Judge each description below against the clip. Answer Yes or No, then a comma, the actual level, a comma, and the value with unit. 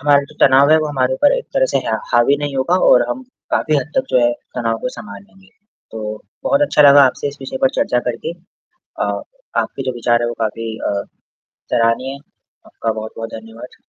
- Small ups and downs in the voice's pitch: No, average, 4.0 semitones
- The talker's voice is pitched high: No, low, 125 Hz